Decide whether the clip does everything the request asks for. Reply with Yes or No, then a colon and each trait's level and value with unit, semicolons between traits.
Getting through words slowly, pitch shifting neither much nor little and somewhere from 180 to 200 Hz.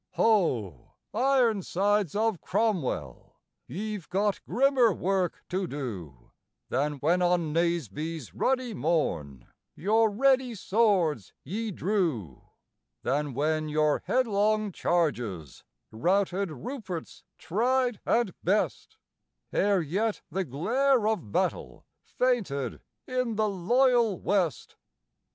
No: slow, 100 wpm; wide, 6.7 semitones; high, 190 Hz